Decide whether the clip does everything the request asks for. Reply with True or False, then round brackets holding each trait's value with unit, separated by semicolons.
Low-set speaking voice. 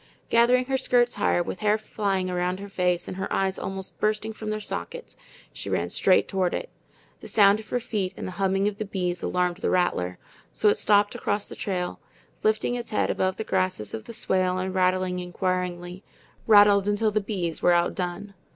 False (195 Hz)